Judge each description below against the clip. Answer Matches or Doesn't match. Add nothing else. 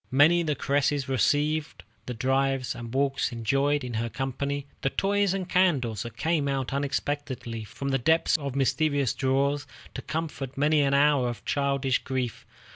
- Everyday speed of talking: Matches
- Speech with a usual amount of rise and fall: Doesn't match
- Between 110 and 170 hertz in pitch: Matches